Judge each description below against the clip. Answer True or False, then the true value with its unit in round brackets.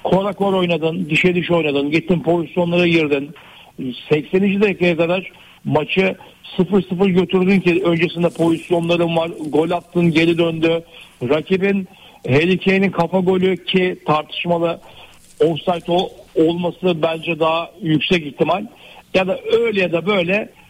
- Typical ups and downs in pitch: False (2.3 semitones)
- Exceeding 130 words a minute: False (120 wpm)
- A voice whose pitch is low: False (175 Hz)